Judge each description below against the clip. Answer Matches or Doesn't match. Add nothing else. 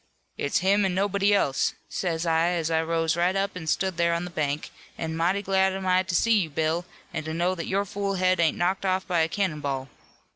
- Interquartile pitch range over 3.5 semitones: Doesn't match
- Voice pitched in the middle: Matches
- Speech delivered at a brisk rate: Matches